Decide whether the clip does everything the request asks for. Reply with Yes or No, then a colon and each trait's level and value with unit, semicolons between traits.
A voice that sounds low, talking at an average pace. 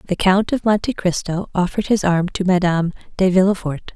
No: medium, 185 Hz; average, 180 wpm